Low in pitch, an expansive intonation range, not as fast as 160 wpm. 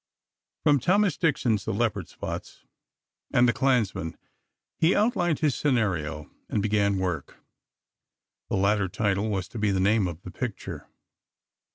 Yes: low, 105 Hz; wide, 5.9 semitones; average, 140 wpm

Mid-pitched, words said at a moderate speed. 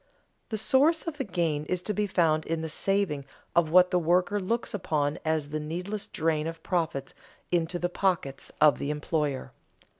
Yes: medium, 170 Hz; average, 180 wpm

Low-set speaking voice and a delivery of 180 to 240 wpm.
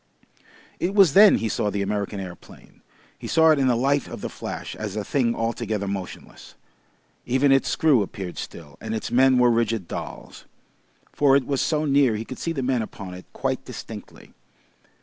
Yes: low, 120 Hz; average, 190 wpm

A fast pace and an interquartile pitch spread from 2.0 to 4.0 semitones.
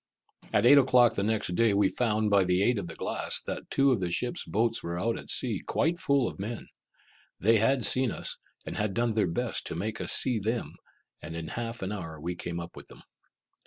No: fast, 230 wpm; average, 4.5 semitones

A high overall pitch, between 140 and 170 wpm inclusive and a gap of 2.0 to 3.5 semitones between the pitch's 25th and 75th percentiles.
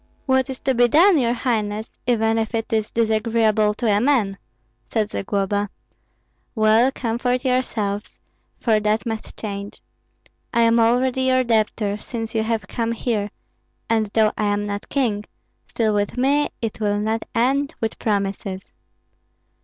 Yes: high, 225 Hz; average, 150 wpm; narrow, 2.6 semitones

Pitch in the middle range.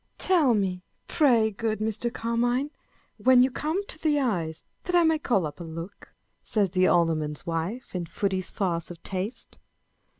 No: high, 215 Hz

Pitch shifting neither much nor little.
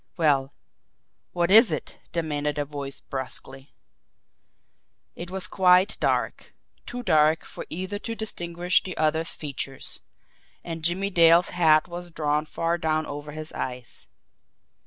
Yes: average, 3.0 semitones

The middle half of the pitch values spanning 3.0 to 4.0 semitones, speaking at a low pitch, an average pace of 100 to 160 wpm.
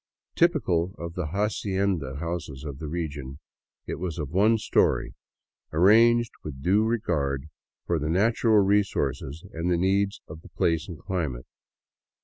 No: average, 4.7 semitones; very low, 85 Hz; average, 140 wpm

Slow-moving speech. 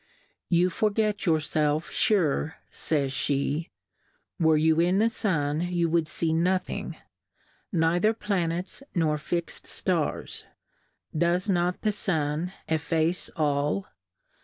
Yes: slow, 105 wpm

